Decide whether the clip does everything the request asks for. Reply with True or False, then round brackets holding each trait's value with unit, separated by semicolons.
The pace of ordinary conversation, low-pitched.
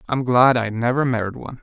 False (220 wpm; 120 Hz)